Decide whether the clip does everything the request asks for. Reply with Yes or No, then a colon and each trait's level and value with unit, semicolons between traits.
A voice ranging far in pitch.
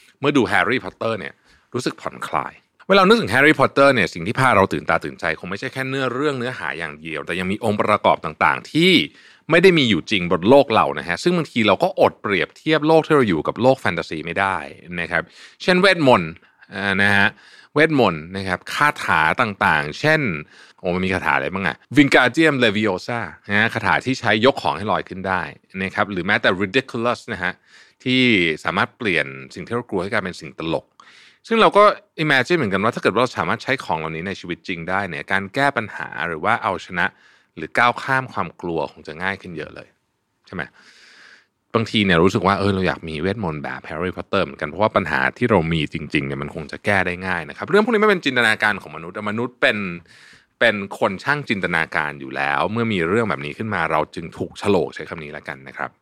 Yes: wide, 7.2 semitones